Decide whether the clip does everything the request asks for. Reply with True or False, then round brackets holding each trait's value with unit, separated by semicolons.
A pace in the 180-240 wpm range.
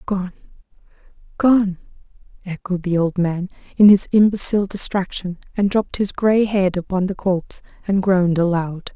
False (140 wpm)